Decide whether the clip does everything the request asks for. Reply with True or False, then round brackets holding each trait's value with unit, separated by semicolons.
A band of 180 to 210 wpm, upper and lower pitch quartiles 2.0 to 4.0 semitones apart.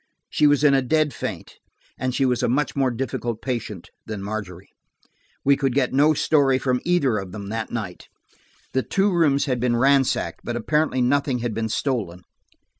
True (185 wpm; 3.7 semitones)